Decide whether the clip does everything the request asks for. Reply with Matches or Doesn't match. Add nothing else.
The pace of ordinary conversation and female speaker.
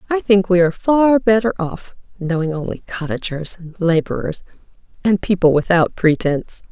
Matches